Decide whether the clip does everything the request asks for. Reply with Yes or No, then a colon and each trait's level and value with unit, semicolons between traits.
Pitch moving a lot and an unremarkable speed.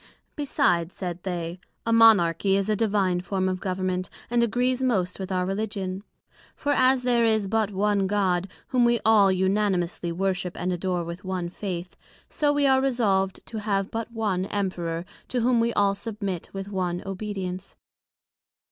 No: average, 3.4 semitones; average, 165 wpm